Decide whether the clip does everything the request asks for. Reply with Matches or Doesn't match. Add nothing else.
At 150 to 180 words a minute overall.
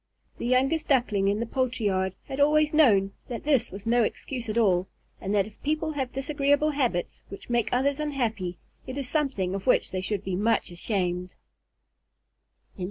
Matches